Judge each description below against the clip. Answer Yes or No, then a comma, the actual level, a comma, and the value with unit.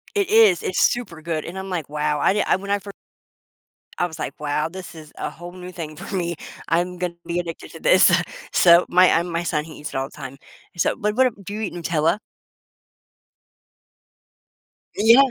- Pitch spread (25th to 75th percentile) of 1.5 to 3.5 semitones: Yes, average, 3.1 semitones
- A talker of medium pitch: Yes, medium, 175 Hz